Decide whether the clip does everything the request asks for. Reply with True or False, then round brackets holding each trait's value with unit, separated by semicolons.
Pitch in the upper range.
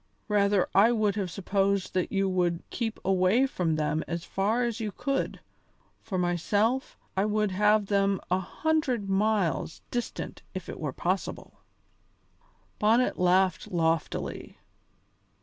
True (195 Hz)